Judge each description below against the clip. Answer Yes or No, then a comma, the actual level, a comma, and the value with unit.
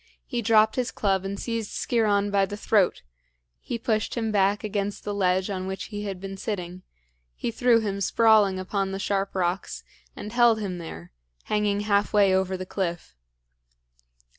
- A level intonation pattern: Yes, narrow, 2.1 semitones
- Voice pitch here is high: Yes, high, 200 Hz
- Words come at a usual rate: Yes, average, 170 wpm